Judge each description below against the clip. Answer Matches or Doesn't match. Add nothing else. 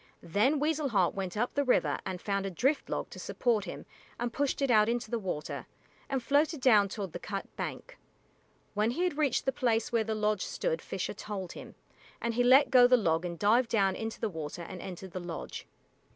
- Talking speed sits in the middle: Doesn't match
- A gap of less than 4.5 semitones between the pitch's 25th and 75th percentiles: Doesn't match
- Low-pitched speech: Doesn't match